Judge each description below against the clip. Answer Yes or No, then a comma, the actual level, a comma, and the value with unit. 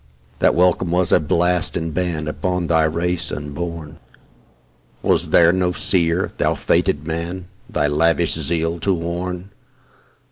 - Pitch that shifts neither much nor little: No, narrow, 1.7 semitones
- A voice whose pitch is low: Yes, very low, 85 Hz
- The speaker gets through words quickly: No, slow, 135 wpm